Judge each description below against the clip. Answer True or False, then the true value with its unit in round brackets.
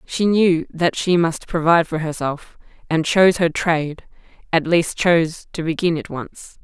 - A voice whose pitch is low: False (165 Hz)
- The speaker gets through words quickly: False (170 wpm)